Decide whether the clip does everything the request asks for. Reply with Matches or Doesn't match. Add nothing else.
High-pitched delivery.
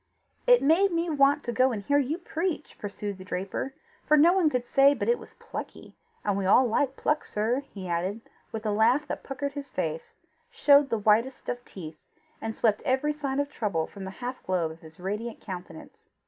Matches